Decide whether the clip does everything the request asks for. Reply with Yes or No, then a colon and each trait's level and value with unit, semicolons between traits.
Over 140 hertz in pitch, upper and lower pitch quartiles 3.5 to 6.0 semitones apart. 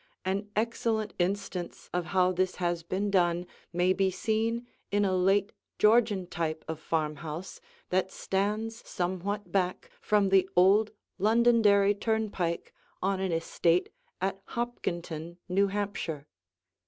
No: high, 190 Hz; average, 2.8 semitones